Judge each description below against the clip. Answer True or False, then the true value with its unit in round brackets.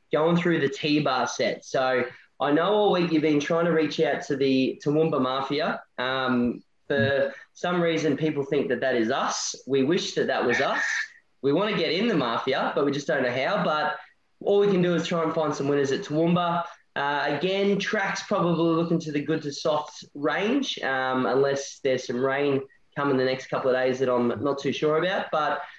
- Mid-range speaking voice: True (150 Hz)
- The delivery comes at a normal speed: False (210 wpm)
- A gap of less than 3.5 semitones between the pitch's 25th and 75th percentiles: False (4.1 semitones)